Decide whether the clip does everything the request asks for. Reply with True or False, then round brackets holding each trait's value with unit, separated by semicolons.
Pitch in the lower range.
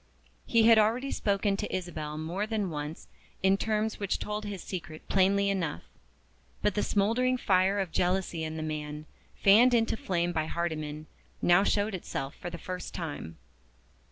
False (190 Hz)